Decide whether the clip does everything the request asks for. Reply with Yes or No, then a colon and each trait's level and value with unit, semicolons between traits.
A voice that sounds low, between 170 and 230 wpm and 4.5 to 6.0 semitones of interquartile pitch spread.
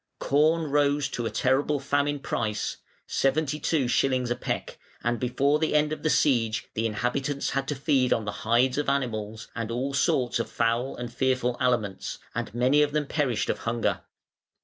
No: low, 130 Hz; average, 180 wpm; average, 3.4 semitones